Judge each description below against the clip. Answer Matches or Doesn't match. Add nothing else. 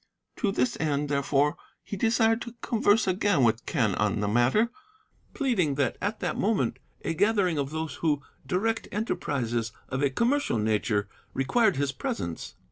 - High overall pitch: Doesn't match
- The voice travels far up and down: Matches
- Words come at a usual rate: Matches